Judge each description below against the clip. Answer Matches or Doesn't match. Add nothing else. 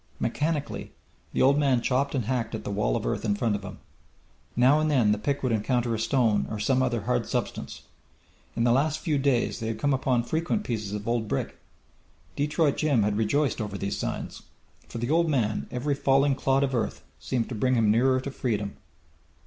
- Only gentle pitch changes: Doesn't match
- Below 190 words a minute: Doesn't match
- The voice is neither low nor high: Doesn't match